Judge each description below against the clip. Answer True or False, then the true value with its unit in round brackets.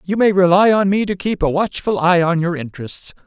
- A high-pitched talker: False (180 Hz)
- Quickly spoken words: True (240 wpm)